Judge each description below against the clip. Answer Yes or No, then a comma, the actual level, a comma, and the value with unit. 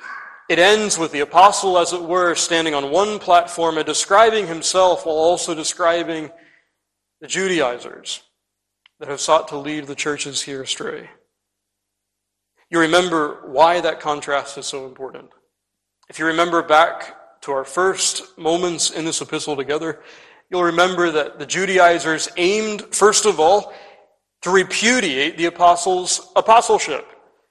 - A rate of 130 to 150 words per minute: Yes, slow, 135 wpm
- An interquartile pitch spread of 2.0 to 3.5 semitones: No, average, 3.9 semitones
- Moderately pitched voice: Yes, medium, 170 Hz